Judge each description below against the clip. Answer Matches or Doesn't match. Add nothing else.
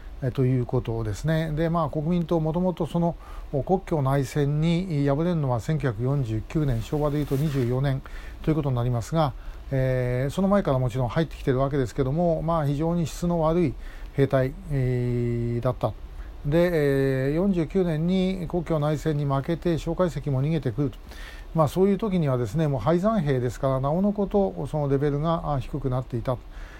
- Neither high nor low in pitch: Matches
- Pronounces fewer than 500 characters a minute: Matches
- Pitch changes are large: Doesn't match